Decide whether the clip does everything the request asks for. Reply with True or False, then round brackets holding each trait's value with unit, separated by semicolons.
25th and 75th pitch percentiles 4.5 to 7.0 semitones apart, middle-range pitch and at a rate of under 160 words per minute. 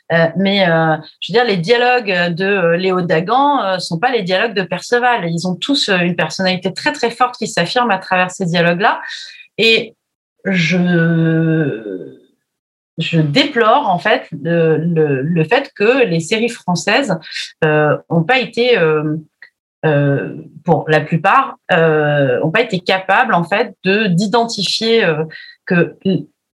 True (5.3 semitones; 180 Hz; 150 wpm)